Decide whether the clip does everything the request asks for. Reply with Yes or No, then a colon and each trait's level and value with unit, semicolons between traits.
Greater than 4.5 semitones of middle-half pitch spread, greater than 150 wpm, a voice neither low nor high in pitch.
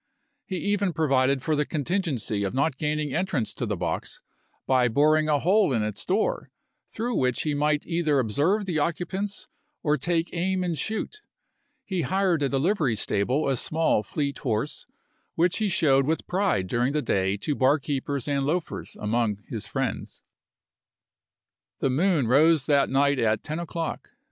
Yes: average, 4.9 semitones; average, 165 wpm; medium, 150 Hz